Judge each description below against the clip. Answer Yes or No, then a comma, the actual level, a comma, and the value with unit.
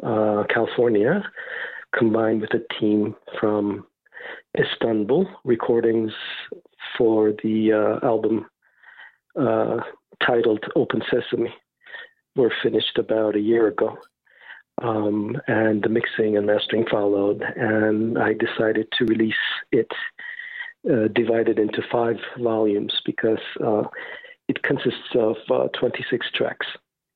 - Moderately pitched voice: No, low, 110 Hz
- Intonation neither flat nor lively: No, narrow, 1.5 semitones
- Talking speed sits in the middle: No, slow, 110 wpm